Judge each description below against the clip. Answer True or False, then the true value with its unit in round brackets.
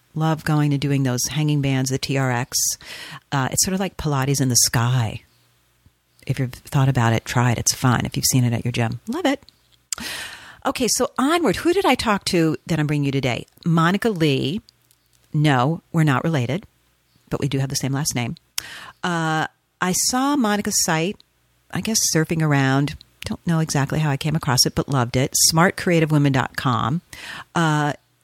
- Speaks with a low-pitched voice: False (145 Hz)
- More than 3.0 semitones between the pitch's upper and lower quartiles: True (4.9 semitones)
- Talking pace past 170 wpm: True (180 wpm)